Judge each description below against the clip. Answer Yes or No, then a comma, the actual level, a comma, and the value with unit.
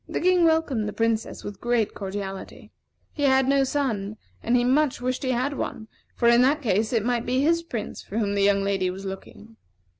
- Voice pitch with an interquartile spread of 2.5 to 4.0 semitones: No, average, 4.7 semitones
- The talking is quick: Yes, fast, 210 wpm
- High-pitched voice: Yes, high, 235 Hz